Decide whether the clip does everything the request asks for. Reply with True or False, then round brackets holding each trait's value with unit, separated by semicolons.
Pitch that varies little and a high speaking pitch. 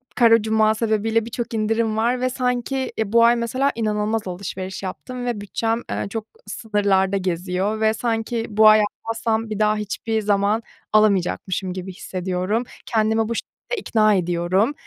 True (2.3 semitones; 220 Hz)